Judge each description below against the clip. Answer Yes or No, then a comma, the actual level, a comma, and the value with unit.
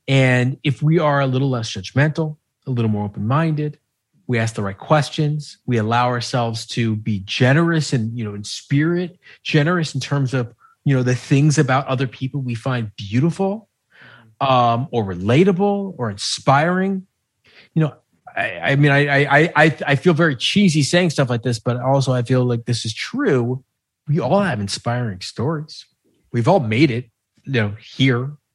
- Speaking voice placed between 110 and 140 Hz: Yes, low, 135 Hz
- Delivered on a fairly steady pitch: No, average, 4.4 semitones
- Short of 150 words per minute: No, average, 175 wpm